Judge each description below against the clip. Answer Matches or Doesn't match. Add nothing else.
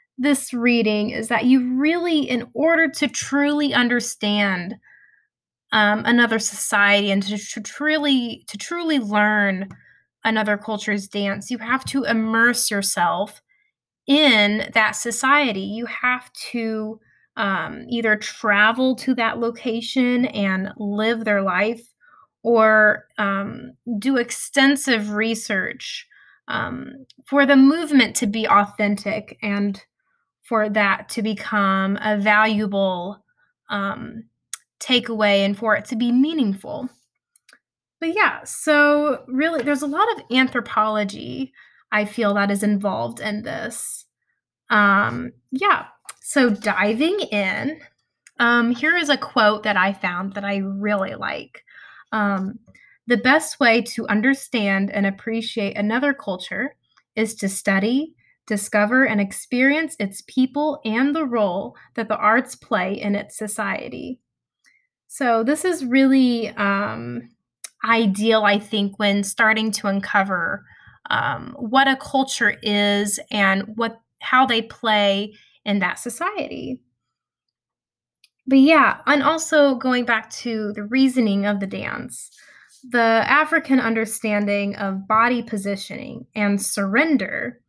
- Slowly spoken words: Matches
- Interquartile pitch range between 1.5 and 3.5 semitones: Doesn't match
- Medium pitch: Doesn't match